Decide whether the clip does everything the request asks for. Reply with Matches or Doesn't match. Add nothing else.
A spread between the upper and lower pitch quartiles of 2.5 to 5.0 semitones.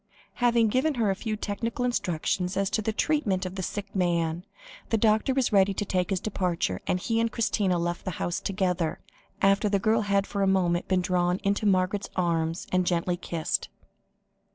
Matches